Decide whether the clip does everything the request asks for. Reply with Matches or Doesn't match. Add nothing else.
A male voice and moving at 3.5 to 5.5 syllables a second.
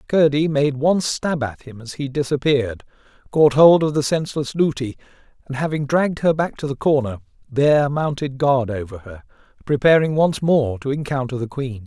Matches